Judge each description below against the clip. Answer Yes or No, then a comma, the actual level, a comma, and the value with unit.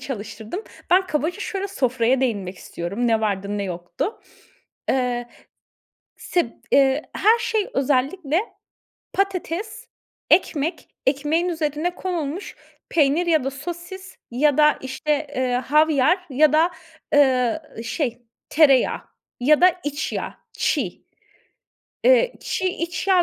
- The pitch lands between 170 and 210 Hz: No, very high, 300 Hz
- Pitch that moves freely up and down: Yes, wide, 5.8 semitones